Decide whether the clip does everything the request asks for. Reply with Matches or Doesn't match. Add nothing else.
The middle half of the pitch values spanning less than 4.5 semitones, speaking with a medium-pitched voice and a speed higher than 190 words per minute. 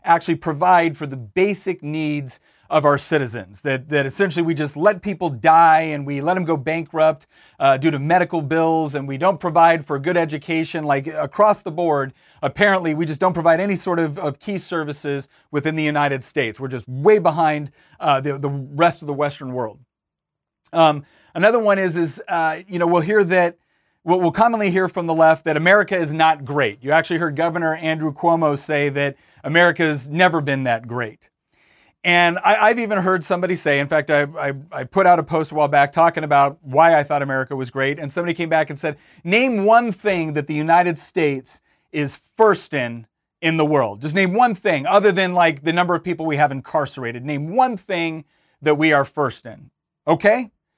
Matches